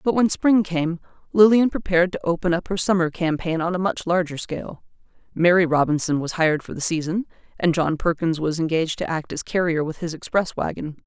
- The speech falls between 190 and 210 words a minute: Yes, average, 200 wpm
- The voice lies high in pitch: No, medium, 170 Hz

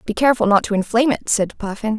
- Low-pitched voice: No, high, 220 Hz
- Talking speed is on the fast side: Yes, fast, 240 wpm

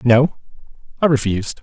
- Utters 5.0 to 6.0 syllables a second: Yes, 5.6 syllables/s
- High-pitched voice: No, low, 125 Hz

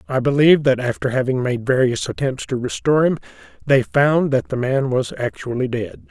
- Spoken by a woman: No, male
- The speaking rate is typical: Yes, average, 185 wpm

